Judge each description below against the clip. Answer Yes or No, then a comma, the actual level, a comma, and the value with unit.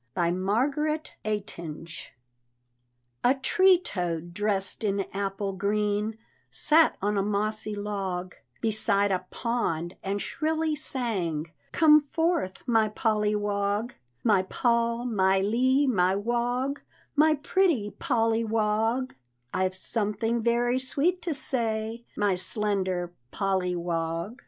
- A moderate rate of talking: No, slow, 115 wpm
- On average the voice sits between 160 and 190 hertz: No, high, 215 Hz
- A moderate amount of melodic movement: Yes, average, 4.1 semitones